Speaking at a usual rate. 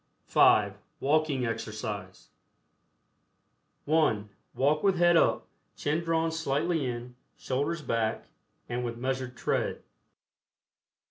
No: slow, 95 wpm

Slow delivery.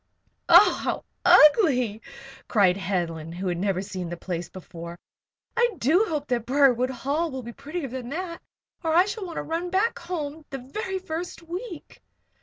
No: average, 170 wpm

